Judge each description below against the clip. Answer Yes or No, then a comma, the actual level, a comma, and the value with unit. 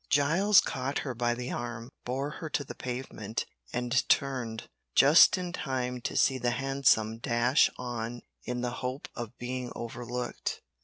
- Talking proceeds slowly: No, average, 155 wpm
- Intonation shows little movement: Yes, narrow, 2.1 semitones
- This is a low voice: Yes, low, 125 Hz